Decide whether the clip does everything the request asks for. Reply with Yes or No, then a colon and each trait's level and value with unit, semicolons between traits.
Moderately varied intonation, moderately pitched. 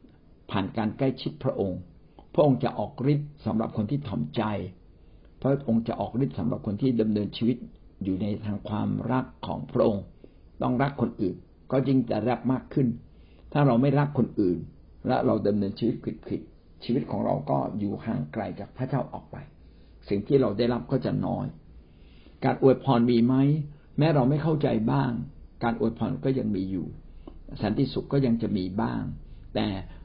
No: average, 4.7 semitones; low, 115 Hz